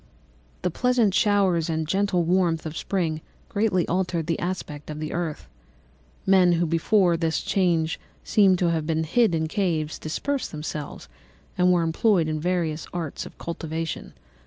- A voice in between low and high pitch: Yes, medium, 170 Hz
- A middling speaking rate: Yes, average, 155 wpm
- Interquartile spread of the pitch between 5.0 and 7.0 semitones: No, average, 2.8 semitones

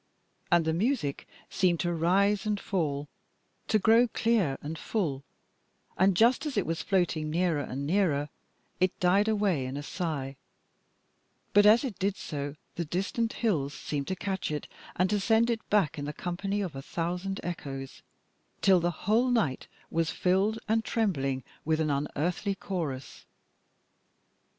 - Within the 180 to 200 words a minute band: No, average, 155 wpm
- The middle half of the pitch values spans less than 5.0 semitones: No, wide, 5.5 semitones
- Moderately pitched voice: Yes, medium, 180 Hz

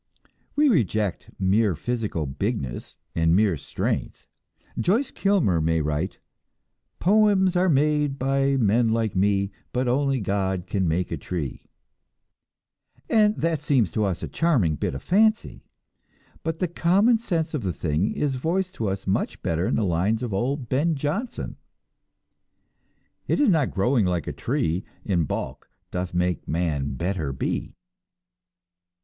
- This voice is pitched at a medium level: No, low, 110 Hz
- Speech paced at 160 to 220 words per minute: No, average, 145 wpm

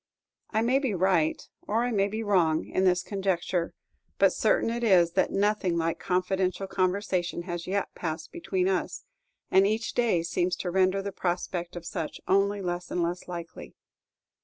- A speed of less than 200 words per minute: Yes, average, 170 wpm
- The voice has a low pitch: No, medium, 185 Hz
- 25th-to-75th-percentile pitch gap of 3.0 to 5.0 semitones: No, narrow, 2.5 semitones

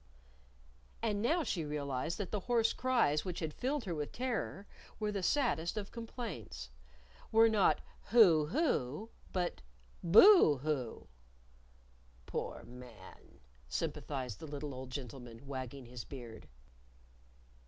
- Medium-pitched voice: Yes, medium, 160 Hz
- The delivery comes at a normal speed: No, slow, 120 wpm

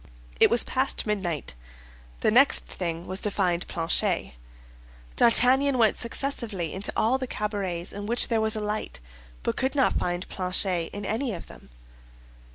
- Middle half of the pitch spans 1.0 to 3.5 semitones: No, average, 4.7 semitones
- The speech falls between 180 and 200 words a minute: No, average, 160 wpm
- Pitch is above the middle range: Yes, high, 210 Hz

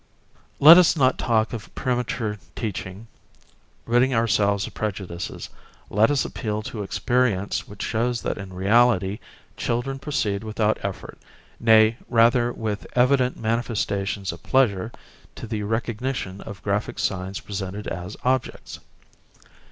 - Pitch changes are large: No, average, 3.4 semitones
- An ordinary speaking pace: No, slow, 125 wpm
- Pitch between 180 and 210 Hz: No, low, 110 Hz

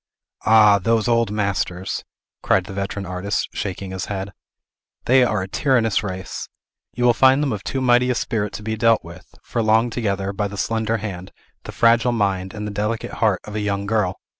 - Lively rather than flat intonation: No, average, 2.8 semitones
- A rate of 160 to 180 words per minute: No, average, 195 wpm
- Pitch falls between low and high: No, low, 105 Hz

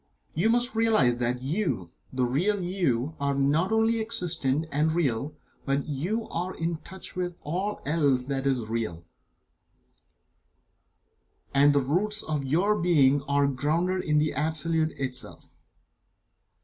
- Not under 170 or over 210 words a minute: No, average, 140 wpm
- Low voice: No, medium, 150 Hz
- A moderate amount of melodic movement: Yes, average, 4.9 semitones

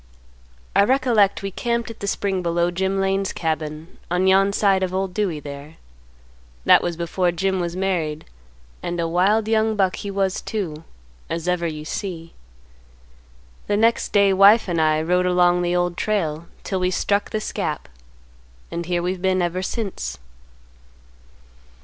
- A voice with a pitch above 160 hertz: Yes, medium, 185 Hz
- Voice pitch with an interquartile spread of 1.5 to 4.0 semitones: Yes, narrow, 2.6 semitones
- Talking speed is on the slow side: No, average, 160 wpm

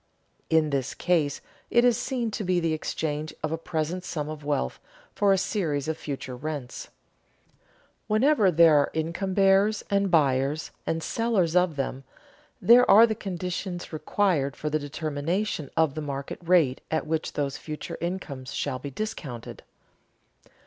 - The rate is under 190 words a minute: Yes, average, 155 wpm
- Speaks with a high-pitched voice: No, medium, 160 Hz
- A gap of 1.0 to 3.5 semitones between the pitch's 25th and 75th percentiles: No, average, 4.7 semitones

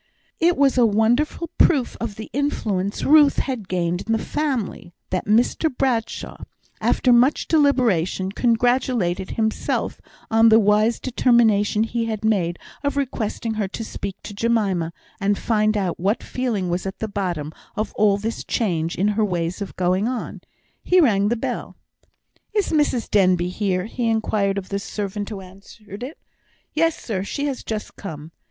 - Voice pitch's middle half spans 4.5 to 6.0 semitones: No, average, 3.9 semitones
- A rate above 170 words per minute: No, average, 160 wpm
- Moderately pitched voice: No, high, 215 Hz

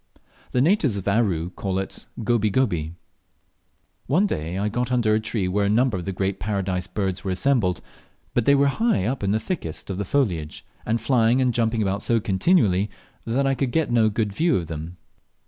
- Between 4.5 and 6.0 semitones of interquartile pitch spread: Yes, average, 4.8 semitones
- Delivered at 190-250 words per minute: Yes, average, 200 wpm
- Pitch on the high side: No, low, 105 Hz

